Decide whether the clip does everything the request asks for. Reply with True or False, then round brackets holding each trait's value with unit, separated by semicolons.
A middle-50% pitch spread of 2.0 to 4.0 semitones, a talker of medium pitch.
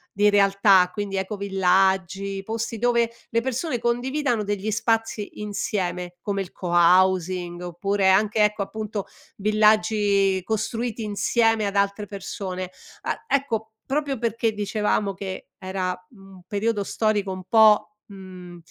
False (2.5 semitones; 205 Hz)